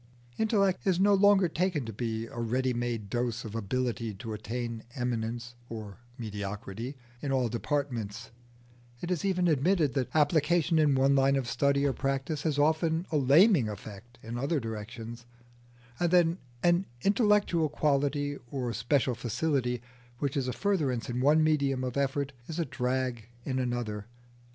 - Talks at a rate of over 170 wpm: No, average, 155 wpm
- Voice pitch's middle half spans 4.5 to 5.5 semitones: Yes, average, 4.8 semitones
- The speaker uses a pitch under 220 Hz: Yes, low, 135 Hz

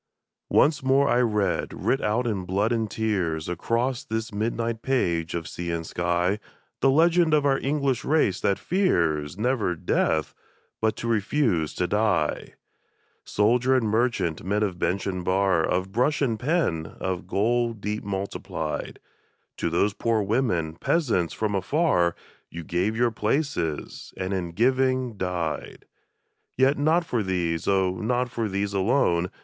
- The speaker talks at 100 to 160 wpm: Yes, average, 150 wpm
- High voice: No, low, 105 Hz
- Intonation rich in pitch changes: Yes, wide, 5.7 semitones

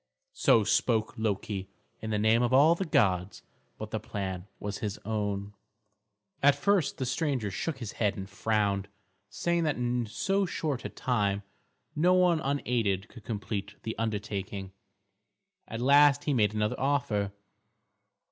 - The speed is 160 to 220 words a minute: No, average, 145 wpm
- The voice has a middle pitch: No, low, 110 Hz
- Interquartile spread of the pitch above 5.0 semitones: Yes, wide, 5.4 semitones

